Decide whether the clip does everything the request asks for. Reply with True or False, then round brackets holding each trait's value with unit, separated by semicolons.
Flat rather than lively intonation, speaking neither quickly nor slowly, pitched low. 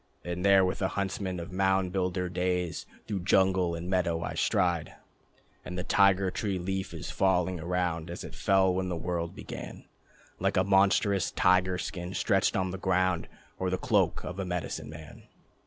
True (1.3 semitones; 175 wpm; 90 Hz)